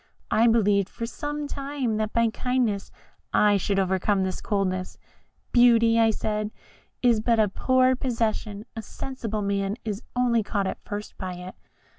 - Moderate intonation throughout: Yes, average, 3.0 semitones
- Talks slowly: No, average, 155 wpm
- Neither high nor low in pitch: No, high, 215 Hz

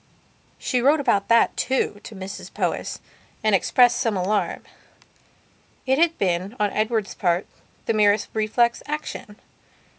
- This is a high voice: Yes, high, 215 Hz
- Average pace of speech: No, slow, 130 wpm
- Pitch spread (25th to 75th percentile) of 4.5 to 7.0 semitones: No, average, 3.5 semitones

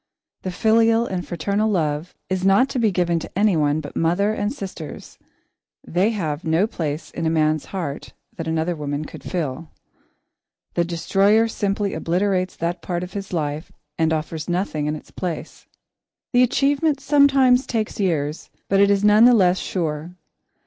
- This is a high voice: No, medium, 180 Hz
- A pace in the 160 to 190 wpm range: Yes, average, 165 wpm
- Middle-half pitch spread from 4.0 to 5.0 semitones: Yes, average, 4.5 semitones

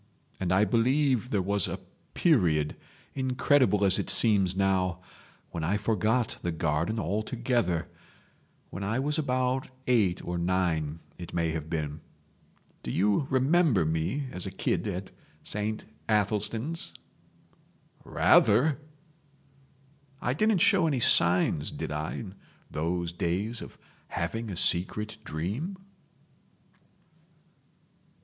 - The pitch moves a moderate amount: No, wide, 6.5 semitones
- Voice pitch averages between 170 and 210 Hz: No, low, 100 Hz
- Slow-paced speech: Yes, slow, 110 wpm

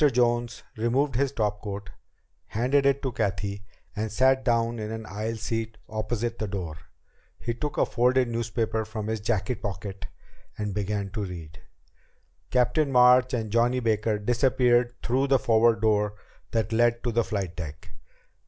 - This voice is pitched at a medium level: No, low, 115 Hz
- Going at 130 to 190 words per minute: Yes, average, 155 wpm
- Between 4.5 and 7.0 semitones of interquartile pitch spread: No, average, 2.8 semitones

